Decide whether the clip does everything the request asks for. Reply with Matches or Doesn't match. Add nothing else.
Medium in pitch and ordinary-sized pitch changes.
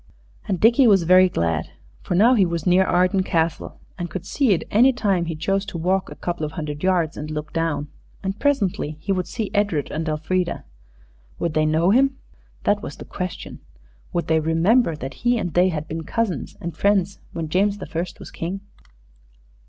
Matches